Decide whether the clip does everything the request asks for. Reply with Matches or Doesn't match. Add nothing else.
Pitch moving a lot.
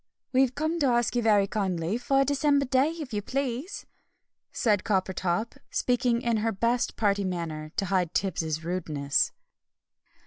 Matches